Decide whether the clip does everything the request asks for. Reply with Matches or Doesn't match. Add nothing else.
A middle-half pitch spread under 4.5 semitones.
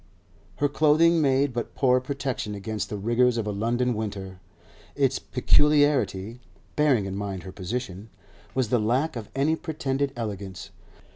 Doesn't match